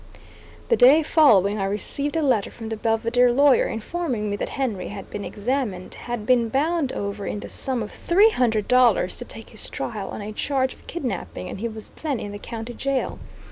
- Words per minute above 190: Yes, fast, 205 wpm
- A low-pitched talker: No, high, 235 Hz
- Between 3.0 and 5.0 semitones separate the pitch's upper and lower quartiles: Yes, average, 4.7 semitones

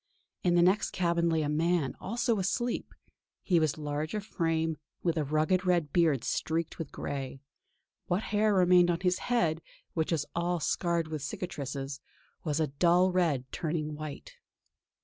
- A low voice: No, medium, 165 Hz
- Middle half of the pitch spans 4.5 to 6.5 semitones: No, average, 2.9 semitones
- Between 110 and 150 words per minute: No, average, 160 wpm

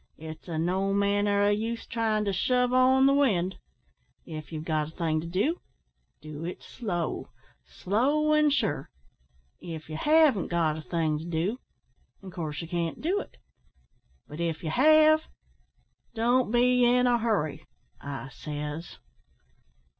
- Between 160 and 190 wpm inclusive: No, average, 150 wpm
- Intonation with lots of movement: Yes, wide, 7.6 semitones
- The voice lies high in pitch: Yes, high, 195 Hz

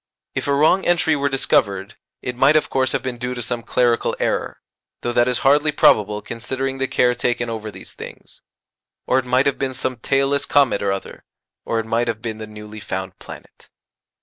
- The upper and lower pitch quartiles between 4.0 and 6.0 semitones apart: No, average, 3.4 semitones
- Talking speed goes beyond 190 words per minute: Yes, average, 200 wpm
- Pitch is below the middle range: Yes, low, 125 Hz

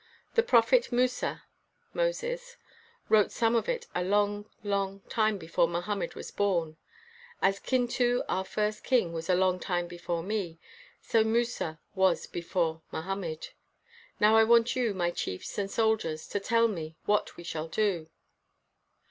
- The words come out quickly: No, average, 150 wpm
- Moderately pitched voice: No, high, 200 Hz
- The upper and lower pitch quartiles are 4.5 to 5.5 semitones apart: Yes, average, 4.9 semitones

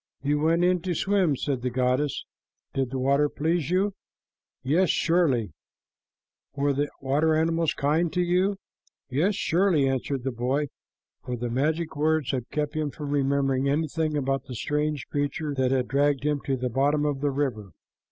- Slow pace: No, average, 170 wpm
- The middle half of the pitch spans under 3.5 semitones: Yes, average, 3.0 semitones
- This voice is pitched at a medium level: Yes, medium, 145 Hz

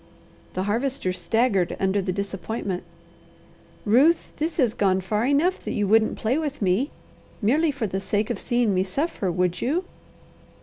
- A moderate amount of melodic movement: No, wide, 6.0 semitones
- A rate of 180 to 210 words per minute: No, average, 160 wpm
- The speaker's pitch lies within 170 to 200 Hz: No, high, 215 Hz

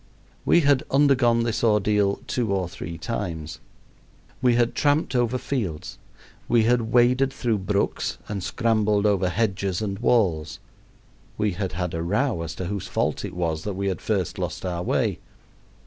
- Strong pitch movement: No, average, 4.6 semitones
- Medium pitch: No, low, 105 Hz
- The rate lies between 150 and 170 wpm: Yes, average, 165 wpm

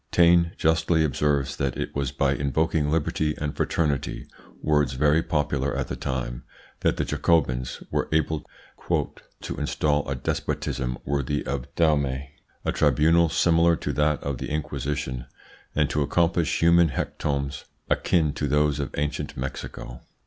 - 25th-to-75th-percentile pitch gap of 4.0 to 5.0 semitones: No, narrow, 2.4 semitones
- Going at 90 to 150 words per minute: Yes, average, 140 wpm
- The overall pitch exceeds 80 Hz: No, very low, 75 Hz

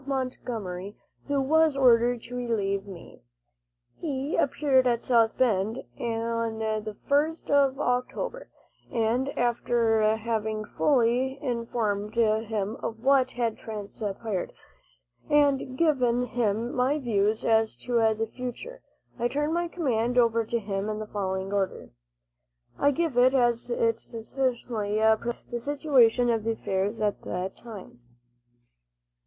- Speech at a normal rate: No, slow, 125 wpm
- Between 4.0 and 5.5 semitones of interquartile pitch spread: No, average, 3.3 semitones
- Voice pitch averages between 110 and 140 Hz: No, high, 235 Hz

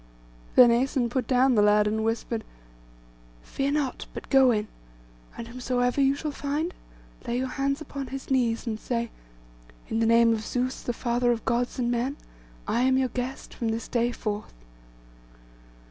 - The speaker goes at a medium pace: Yes, average, 170 wpm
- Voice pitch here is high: Yes, high, 245 Hz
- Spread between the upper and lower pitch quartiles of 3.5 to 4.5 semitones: No, narrow, 2.4 semitones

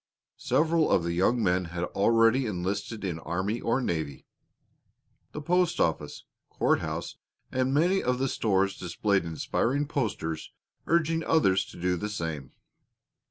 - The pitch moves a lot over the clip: Yes, wide, 7.3 semitones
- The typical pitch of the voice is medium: No, low, 100 Hz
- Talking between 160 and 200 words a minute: No, slow, 135 wpm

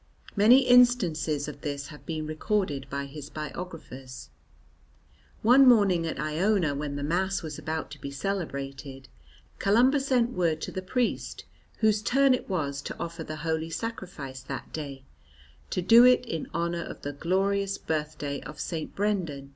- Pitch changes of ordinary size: No, wide, 5.8 semitones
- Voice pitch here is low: No, medium, 165 Hz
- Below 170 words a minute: Yes, average, 155 wpm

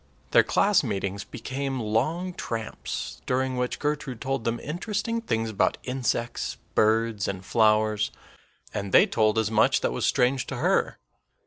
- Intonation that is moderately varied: Yes, average, 3.9 semitones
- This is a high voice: No, low, 115 Hz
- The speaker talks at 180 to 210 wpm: No, average, 145 wpm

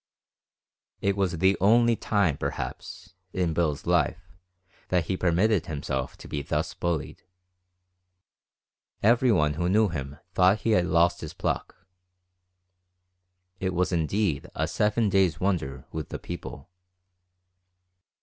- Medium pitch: No, very low, 90 Hz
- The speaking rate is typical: No, slow, 120 wpm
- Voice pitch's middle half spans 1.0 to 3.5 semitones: No, average, 3.9 semitones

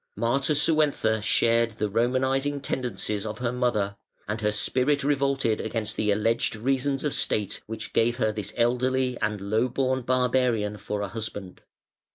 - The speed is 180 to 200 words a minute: No, average, 150 wpm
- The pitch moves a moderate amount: Yes, average, 3.6 semitones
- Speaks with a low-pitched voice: Yes, low, 115 Hz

